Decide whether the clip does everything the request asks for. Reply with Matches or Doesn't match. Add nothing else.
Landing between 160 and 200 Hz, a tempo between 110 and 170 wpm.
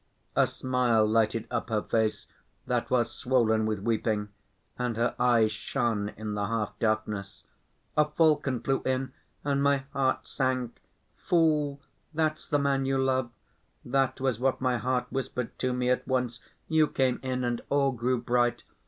Doesn't match